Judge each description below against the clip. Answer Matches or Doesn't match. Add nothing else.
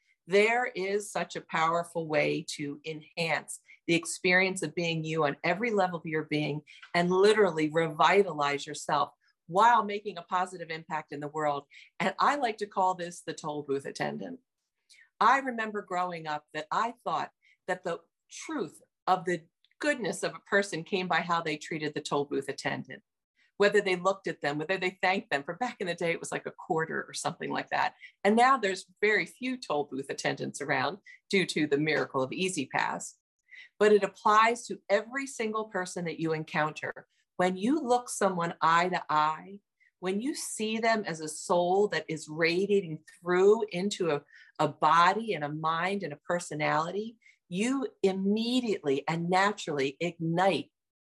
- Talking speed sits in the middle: Matches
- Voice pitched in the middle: Matches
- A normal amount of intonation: Matches